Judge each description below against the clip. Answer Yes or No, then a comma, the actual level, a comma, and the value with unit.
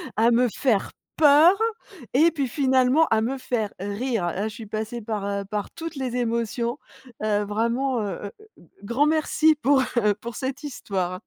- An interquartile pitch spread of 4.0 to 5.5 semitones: Yes, average, 4.5 semitones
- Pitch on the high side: Yes, high, 235 Hz